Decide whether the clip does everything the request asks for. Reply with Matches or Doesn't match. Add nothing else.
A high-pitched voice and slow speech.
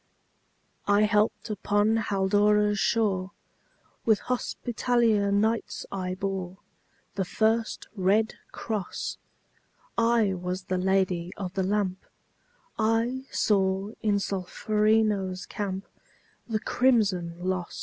Matches